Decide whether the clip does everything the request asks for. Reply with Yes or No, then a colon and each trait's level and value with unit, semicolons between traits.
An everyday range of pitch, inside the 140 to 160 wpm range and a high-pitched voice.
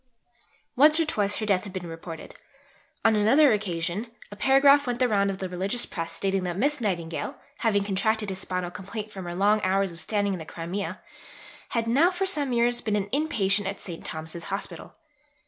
No: average, 4.2 semitones; average, 200 wpm; high, 200 Hz